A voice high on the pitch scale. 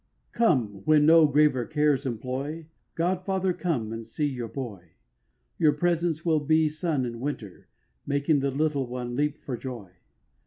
No: medium, 145 Hz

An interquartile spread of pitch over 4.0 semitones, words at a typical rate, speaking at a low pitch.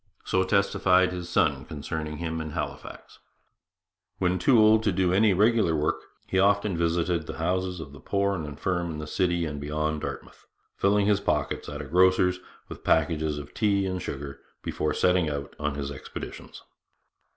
No: average, 3.7 semitones; average, 175 wpm; very low, 85 Hz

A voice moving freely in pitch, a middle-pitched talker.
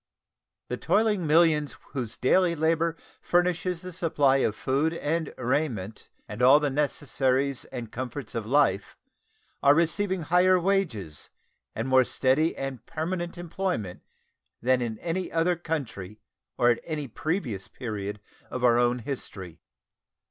Yes: wide, 5.7 semitones; medium, 145 Hz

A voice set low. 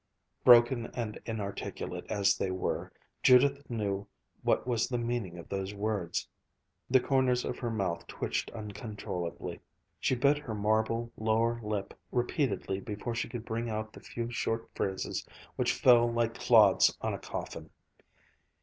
Yes: low, 115 Hz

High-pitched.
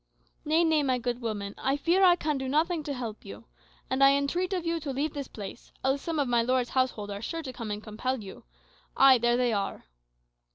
Yes: very high, 260 Hz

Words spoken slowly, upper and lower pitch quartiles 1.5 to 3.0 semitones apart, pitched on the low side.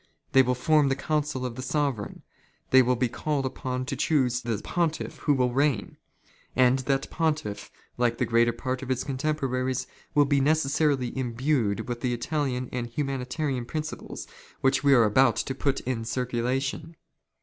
No: average, 175 wpm; narrow, 2.6 semitones; low, 130 Hz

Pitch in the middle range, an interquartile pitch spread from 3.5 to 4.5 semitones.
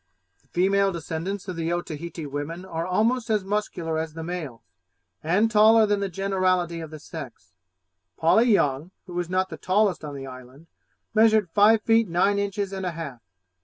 Yes: medium, 180 Hz; average, 3.9 semitones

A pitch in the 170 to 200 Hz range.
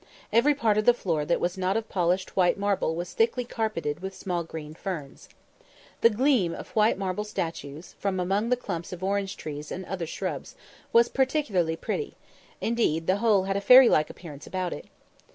Yes: high, 190 Hz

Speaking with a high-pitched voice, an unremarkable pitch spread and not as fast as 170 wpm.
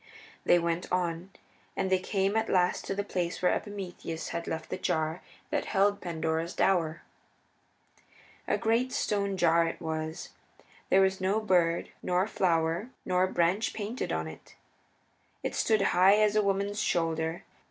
No: medium, 180 Hz; average, 3.2 semitones; average, 150 wpm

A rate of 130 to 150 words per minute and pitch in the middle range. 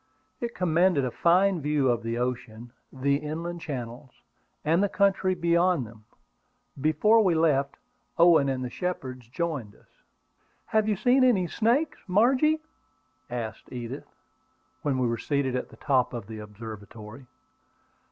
Yes: average, 140 wpm; medium, 145 Hz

